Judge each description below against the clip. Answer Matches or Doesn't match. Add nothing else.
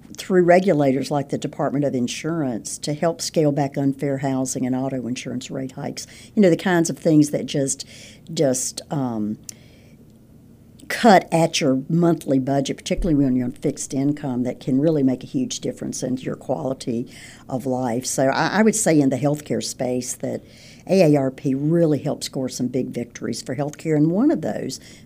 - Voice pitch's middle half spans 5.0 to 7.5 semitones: Doesn't match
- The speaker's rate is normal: Matches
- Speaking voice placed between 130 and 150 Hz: Matches